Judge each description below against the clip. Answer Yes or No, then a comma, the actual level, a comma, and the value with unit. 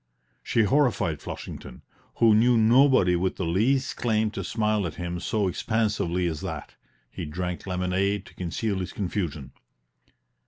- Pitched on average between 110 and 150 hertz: No, low, 100 Hz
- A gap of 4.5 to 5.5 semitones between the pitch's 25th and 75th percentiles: No, average, 3.9 semitones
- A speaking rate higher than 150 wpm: No, average, 145 wpm